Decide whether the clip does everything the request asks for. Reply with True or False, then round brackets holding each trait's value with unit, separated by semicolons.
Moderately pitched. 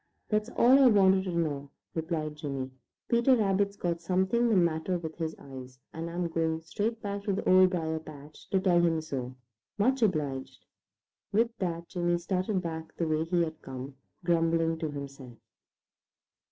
True (170 Hz)